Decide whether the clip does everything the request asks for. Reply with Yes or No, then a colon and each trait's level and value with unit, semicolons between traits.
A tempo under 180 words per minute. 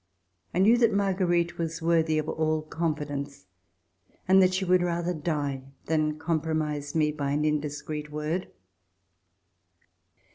Yes: average, 140 wpm